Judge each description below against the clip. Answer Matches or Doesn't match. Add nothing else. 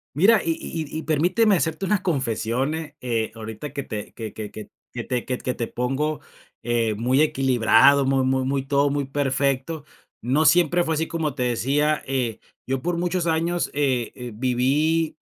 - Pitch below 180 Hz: Matches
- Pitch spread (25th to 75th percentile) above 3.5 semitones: Matches